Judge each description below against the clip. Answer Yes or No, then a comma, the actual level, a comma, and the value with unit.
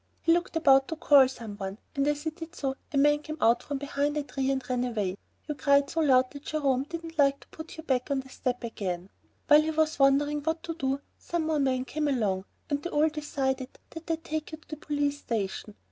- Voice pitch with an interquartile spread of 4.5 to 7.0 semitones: No, average, 2.9 semitones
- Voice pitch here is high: Yes, very high, 285 Hz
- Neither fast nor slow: No, fast, 235 wpm